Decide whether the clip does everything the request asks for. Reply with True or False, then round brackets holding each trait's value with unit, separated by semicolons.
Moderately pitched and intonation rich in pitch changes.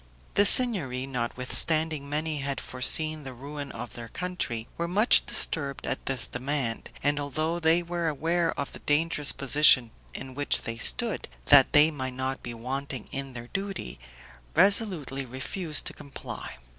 False (145 Hz; 3.8 semitones)